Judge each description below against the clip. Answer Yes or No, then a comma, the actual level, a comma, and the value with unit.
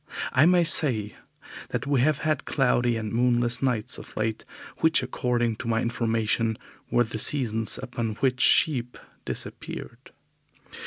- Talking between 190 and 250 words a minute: No, average, 140 wpm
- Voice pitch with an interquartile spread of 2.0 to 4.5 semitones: Yes, average, 2.7 semitones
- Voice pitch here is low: Yes, low, 120 Hz